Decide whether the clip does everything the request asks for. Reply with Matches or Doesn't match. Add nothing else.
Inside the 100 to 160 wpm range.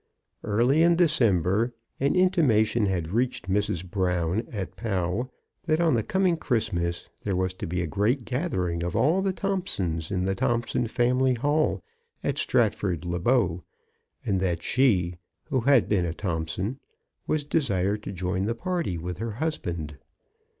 Matches